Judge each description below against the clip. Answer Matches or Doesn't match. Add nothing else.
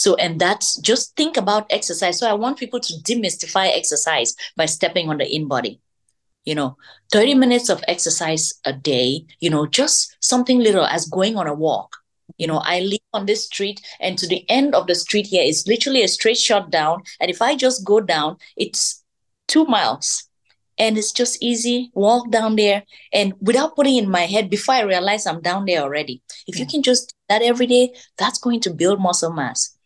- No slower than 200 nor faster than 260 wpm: Matches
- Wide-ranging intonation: Matches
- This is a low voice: Doesn't match